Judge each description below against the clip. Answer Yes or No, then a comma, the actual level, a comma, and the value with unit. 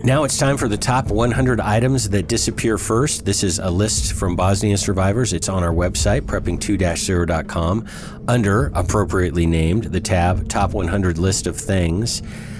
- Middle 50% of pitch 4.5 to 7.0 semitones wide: No, average, 3.8 semitones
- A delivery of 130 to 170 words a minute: Yes, average, 155 wpm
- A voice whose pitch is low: Yes, low, 100 Hz